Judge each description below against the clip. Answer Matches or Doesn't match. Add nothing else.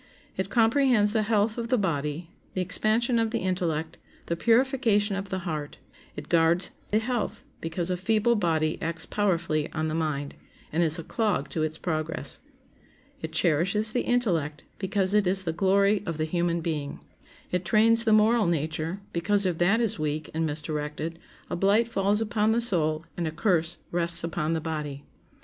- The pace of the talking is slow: Doesn't match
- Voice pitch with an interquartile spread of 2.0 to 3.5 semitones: Doesn't match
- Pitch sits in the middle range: Matches